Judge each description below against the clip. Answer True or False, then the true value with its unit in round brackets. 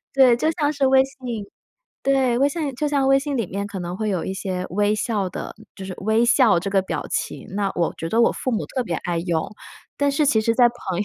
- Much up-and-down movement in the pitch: True (5.8 semitones)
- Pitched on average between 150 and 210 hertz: False (225 Hz)